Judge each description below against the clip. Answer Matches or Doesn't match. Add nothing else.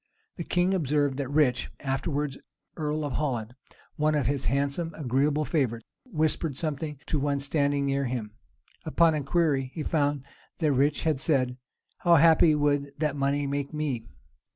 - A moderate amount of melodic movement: Doesn't match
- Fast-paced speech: Doesn't match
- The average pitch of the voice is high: Doesn't match